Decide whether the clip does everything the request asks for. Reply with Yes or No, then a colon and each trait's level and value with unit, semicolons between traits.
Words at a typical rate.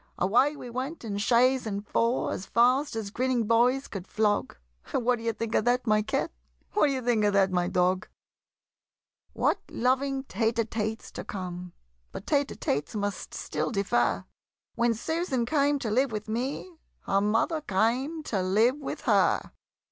Yes: average, 170 wpm